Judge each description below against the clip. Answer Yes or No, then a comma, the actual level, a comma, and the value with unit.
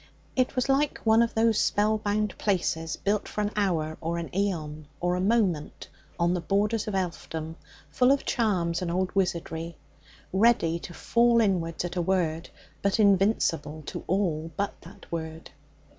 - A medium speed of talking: Yes, average, 165 wpm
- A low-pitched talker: No, medium, 185 Hz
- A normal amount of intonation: Yes, average, 4.2 semitones